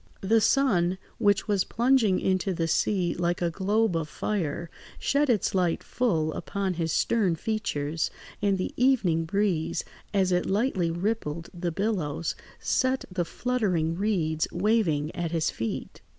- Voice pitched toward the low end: No, medium, 185 Hz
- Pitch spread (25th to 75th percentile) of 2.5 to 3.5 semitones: No, average, 4.4 semitones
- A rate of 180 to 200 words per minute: No, average, 145 wpm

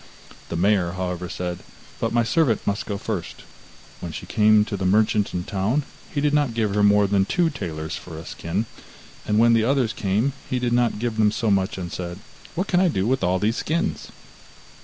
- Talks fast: Yes, fast, 215 wpm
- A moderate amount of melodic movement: Yes, average, 4.3 semitones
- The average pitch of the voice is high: No, low, 105 Hz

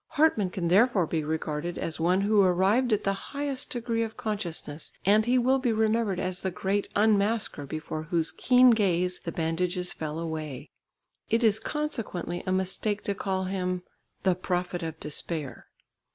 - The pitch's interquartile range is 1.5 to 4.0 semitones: No, average, 4.4 semitones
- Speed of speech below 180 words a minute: Yes, average, 165 wpm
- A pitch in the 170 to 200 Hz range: Yes, high, 190 Hz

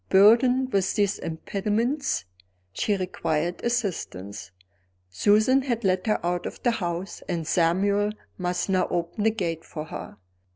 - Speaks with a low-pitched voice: No, high, 195 Hz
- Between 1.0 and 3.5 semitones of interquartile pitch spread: No, average, 4.2 semitones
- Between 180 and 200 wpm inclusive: No, slow, 135 wpm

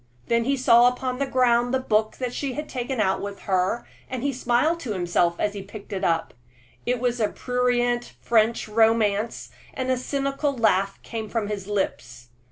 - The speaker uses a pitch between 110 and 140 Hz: No, high, 235 Hz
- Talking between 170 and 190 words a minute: Yes, average, 175 wpm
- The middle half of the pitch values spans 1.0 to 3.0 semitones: No, average, 3.5 semitones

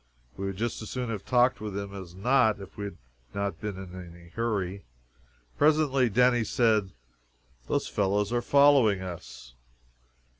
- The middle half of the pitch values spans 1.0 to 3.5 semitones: No, average, 4.1 semitones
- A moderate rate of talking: Yes, average, 155 wpm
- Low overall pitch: Yes, low, 105 Hz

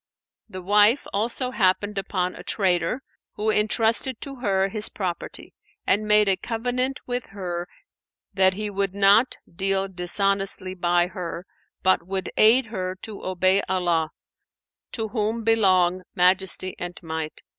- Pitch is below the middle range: No, high, 195 Hz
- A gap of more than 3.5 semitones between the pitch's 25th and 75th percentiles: No, average, 2.8 semitones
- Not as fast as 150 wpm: Yes, slow, 135 wpm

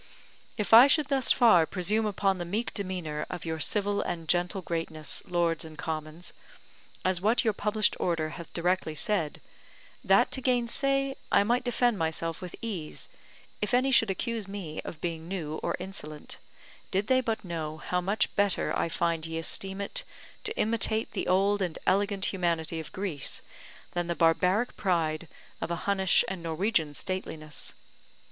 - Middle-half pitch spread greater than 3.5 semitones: Yes, average, 4.3 semitones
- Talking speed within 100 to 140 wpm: No, average, 165 wpm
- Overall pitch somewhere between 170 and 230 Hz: Yes, medium, 185 Hz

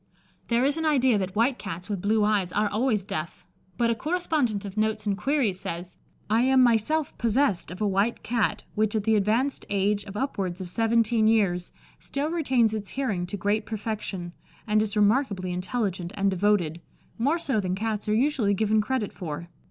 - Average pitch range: Yes, average, 3.4 semitones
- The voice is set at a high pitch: Yes, high, 215 Hz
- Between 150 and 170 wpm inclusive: No, average, 185 wpm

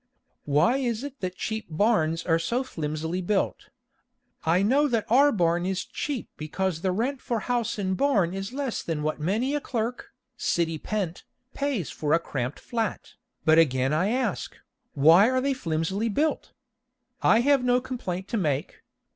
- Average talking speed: Yes, average, 165 wpm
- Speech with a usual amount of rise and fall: No, wide, 7.1 semitones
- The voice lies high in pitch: Yes, high, 195 Hz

